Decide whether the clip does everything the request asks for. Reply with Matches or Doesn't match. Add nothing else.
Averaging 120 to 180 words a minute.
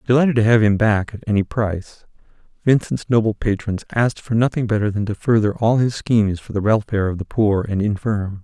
Doesn't match